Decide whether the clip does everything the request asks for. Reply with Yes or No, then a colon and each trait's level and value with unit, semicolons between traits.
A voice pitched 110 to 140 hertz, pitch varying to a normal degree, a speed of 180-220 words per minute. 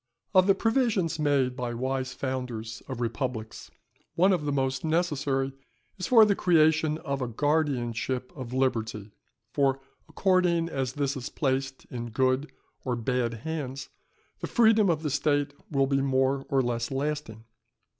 No: low, 135 Hz; average, 3.5 semitones; average, 155 wpm